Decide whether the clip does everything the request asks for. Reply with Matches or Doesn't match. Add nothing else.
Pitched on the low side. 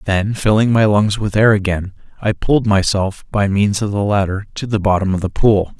Matches